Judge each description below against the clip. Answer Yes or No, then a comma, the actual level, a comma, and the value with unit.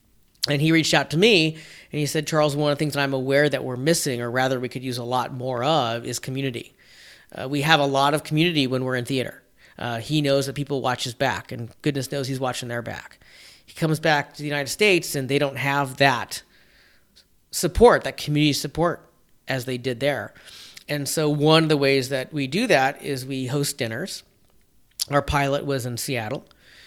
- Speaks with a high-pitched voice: No, medium, 140 Hz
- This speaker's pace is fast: Yes, fast, 215 wpm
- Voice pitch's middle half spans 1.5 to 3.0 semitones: Yes, narrow, 2.5 semitones